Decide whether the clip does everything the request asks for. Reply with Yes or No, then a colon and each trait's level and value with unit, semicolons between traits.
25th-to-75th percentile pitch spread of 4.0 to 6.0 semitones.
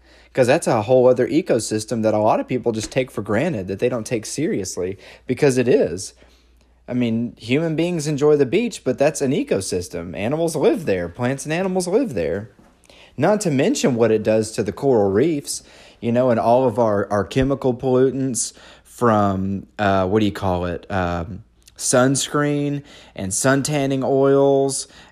Yes: average, 4.7 semitones